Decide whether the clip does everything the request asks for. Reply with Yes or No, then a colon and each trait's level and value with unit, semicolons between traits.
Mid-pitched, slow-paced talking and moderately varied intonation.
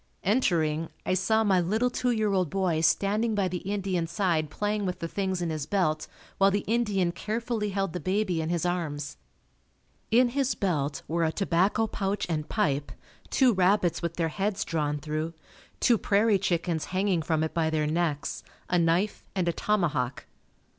No: medium, 180 Hz; average, 175 wpm; average, 4.1 semitones